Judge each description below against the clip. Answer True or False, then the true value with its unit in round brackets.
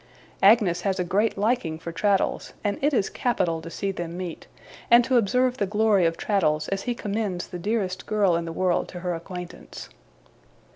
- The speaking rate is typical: True (190 wpm)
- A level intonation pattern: False (3.7 semitones)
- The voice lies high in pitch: True (195 Hz)